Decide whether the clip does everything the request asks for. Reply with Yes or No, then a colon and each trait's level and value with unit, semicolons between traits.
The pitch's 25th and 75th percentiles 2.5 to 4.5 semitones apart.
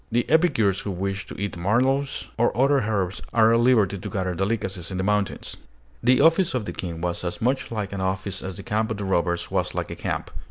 Yes: average, 3.9 semitones